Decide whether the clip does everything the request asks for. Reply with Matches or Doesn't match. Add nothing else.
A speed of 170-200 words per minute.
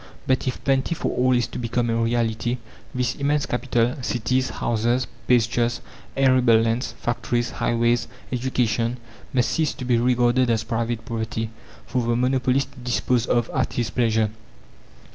Doesn't match